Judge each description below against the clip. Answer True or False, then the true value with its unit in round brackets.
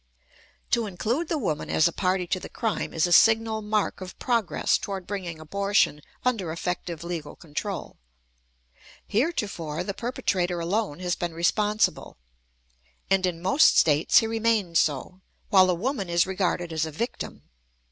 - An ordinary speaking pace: True (150 wpm)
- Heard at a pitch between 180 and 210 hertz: True (185 Hz)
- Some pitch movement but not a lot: True (4.1 semitones)